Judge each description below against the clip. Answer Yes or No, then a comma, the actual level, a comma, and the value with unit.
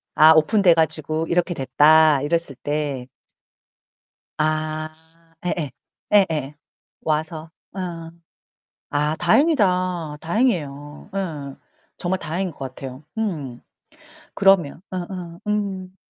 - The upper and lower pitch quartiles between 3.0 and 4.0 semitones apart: Yes, average, 3.5 semitones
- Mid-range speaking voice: Yes, medium, 160 Hz